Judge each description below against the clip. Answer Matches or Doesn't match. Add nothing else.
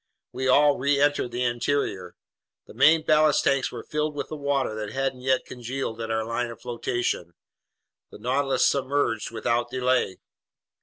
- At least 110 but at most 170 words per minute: Matches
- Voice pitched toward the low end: Matches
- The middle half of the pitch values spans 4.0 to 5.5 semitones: Doesn't match